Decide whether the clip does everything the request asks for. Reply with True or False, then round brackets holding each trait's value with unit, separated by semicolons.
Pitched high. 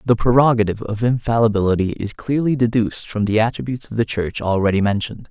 False (110 Hz)